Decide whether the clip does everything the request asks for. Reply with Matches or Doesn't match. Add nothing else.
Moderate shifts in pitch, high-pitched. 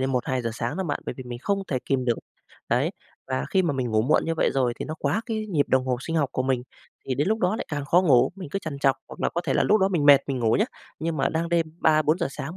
Doesn't match